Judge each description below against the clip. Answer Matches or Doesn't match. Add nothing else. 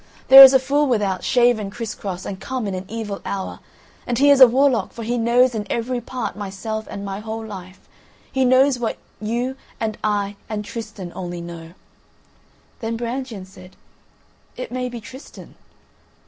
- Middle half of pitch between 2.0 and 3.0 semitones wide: Doesn't match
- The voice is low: Doesn't match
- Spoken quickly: Doesn't match